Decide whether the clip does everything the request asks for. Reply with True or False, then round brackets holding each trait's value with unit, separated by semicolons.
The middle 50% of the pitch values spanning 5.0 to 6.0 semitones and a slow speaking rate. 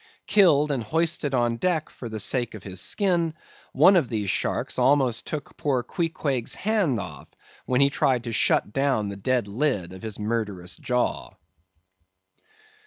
False (5.6 semitones; 160 wpm)